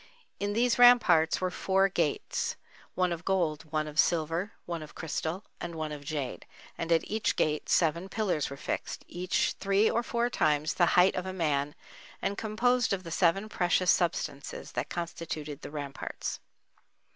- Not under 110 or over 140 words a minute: No, average, 160 wpm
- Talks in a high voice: No, medium, 175 Hz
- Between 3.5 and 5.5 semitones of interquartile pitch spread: Yes, average, 4.0 semitones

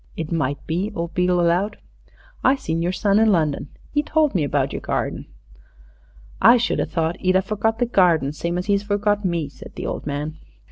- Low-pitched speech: No, medium, 180 Hz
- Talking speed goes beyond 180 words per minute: Yes, average, 200 wpm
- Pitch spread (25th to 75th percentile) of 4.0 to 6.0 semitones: Yes, average, 4.3 semitones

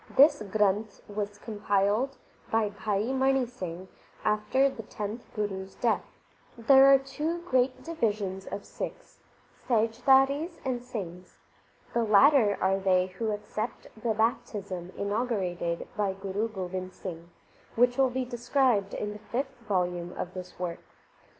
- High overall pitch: Yes, high, 215 Hz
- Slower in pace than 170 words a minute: Yes, slow, 135 wpm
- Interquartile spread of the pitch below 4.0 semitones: No, average, 4.5 semitones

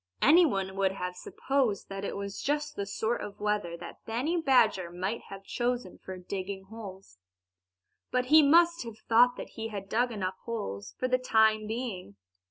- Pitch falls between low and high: No, high, 215 Hz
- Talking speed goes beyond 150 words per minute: Yes, average, 175 wpm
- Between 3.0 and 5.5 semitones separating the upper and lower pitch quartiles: Yes, average, 4.6 semitones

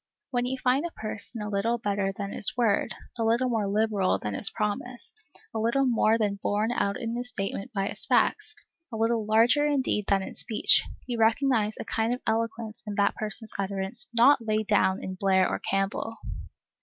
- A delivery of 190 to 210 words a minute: Yes, average, 195 wpm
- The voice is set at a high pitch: Yes, high, 220 Hz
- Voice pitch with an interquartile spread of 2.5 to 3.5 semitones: Yes, average, 2.8 semitones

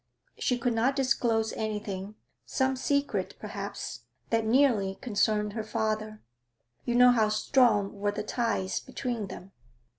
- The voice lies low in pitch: No, high, 220 Hz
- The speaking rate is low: Yes, slow, 130 wpm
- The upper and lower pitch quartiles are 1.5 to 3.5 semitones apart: Yes, average, 2.9 semitones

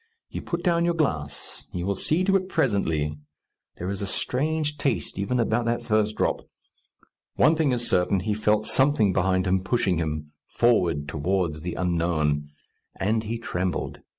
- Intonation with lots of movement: Yes, wide, 6.2 semitones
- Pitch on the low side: Yes, low, 100 Hz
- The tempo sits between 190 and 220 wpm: No, average, 165 wpm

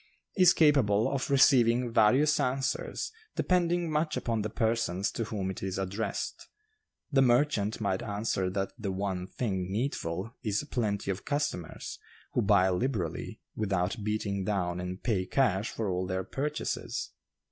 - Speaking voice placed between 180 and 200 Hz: No, low, 105 Hz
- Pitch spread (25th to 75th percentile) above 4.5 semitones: Yes, average, 5.2 semitones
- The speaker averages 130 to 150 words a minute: Yes, average, 145 wpm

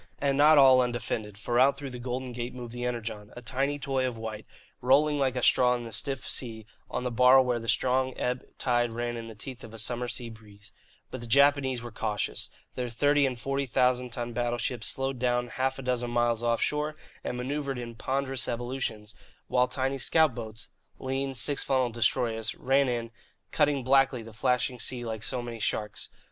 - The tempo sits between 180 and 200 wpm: Yes, average, 195 wpm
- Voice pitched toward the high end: No, low, 125 Hz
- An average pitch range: No, narrow, 2.2 semitones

